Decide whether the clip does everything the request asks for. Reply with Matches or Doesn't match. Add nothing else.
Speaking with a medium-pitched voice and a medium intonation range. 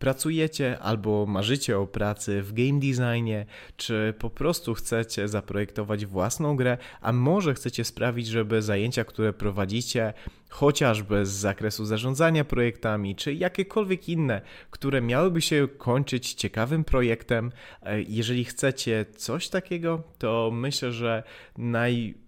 Doesn't match